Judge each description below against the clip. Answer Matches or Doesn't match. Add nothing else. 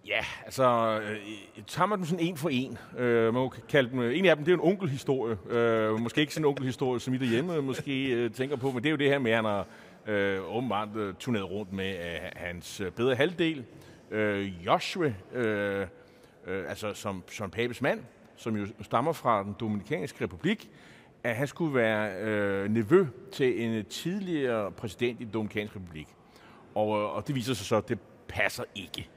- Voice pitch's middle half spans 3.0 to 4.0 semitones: Doesn't match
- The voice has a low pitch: Matches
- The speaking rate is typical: Matches